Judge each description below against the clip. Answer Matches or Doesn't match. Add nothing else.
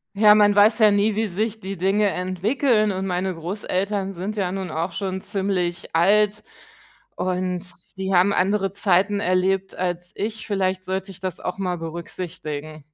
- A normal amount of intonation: Doesn't match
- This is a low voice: Doesn't match